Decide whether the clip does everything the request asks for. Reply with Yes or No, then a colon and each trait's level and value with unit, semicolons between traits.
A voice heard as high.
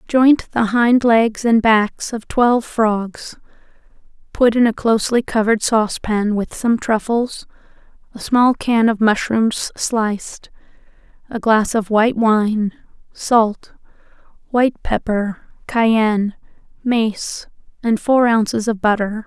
Yes: high, 225 Hz